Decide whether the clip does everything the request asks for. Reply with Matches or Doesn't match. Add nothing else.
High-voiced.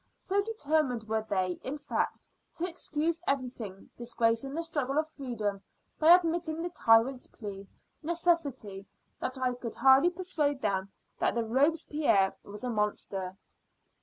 Matches